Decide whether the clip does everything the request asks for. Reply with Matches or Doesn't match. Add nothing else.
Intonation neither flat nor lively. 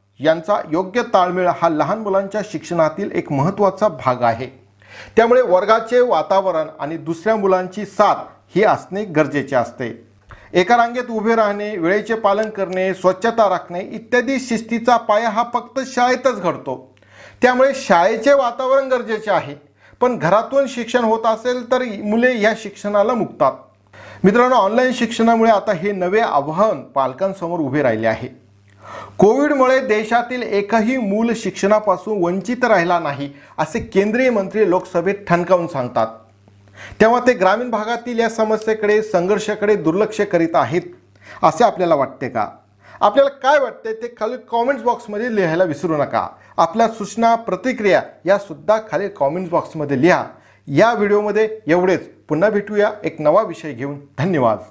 Doesn't match